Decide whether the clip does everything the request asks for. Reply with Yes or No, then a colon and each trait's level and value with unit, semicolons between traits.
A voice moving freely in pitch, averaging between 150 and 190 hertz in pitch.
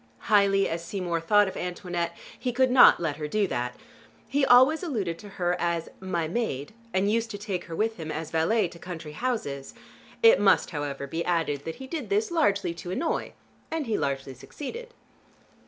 Yes: wide, 6.1 semitones; medium, 185 Hz